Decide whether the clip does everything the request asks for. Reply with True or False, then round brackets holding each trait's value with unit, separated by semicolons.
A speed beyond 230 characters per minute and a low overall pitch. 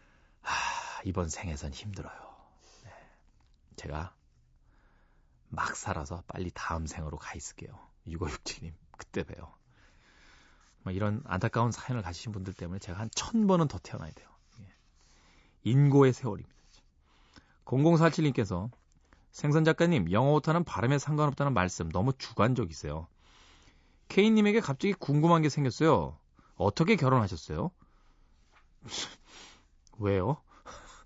True (260 characters per minute; 100 Hz)